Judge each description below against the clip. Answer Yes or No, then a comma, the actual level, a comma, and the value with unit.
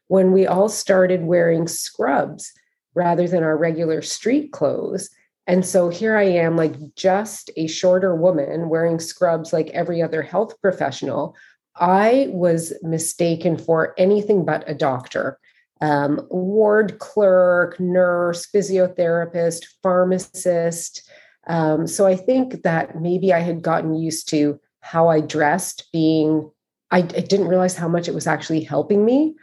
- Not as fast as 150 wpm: Yes, average, 140 wpm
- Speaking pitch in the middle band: Yes, medium, 175 Hz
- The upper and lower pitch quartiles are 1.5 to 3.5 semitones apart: Yes, narrow, 2.5 semitones